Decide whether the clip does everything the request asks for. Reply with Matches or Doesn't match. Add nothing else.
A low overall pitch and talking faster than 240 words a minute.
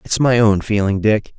Doesn't match